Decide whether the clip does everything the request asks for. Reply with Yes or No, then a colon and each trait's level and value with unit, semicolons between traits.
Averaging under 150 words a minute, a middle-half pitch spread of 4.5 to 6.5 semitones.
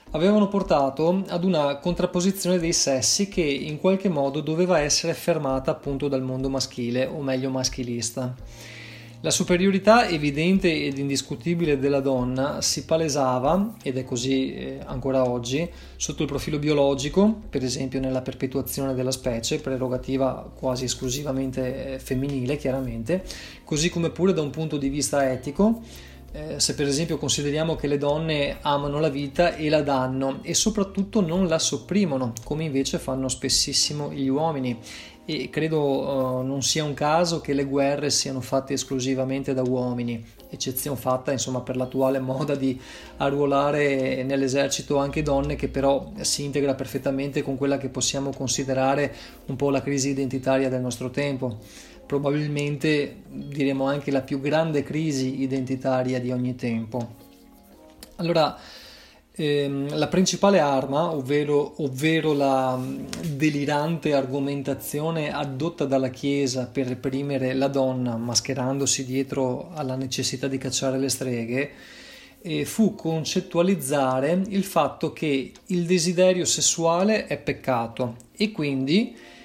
No: average, 135 wpm; average, 2.9 semitones